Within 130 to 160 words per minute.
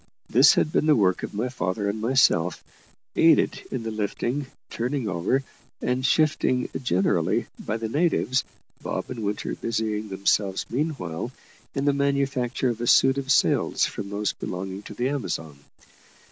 Yes: average, 155 wpm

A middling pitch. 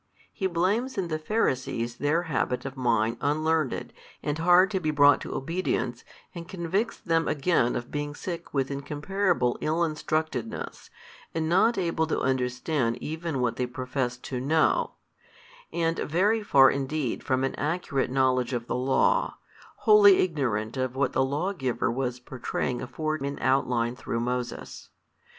Yes: medium, 145 Hz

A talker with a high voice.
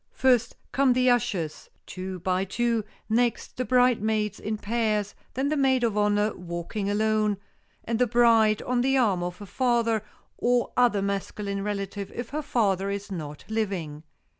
Yes: high, 215 Hz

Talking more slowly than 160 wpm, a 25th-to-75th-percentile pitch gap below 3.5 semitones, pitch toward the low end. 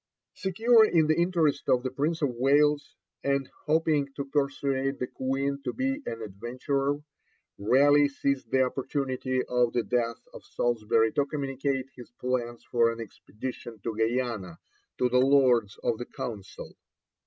Yes: average, 150 wpm; average, 3.0 semitones; low, 130 Hz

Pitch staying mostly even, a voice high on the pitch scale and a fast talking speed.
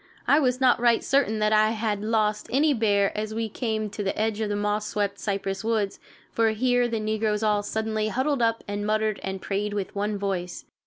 Yes: narrow, 1.7 semitones; high, 215 Hz; fast, 210 wpm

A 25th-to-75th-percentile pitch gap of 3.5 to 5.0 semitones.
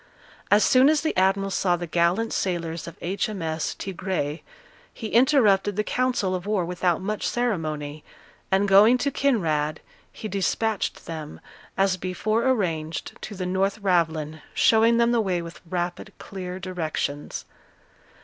Yes: average, 4.2 semitones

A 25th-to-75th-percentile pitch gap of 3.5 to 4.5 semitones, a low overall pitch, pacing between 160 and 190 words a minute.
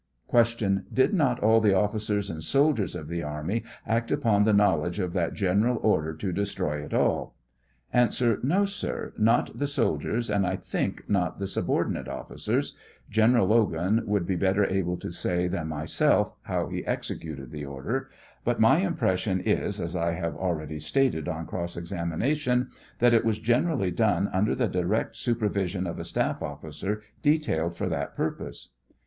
No: average, 5.2 semitones; low, 100 Hz; average, 170 wpm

